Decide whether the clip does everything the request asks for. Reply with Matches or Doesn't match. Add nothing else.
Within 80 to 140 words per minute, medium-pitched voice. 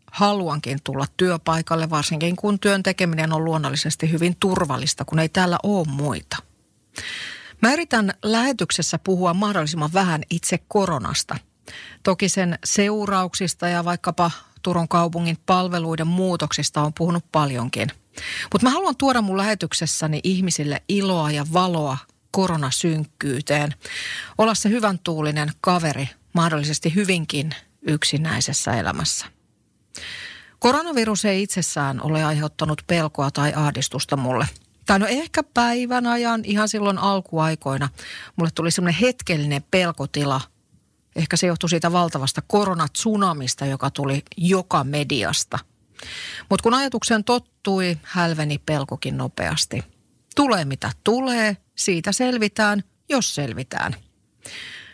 Matches